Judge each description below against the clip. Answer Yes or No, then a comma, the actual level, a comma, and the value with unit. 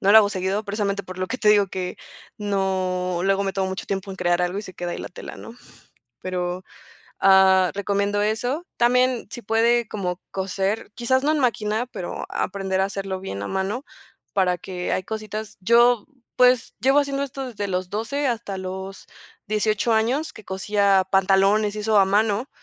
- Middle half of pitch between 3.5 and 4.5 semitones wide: No, average, 2.9 semitones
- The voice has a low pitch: No, high, 200 Hz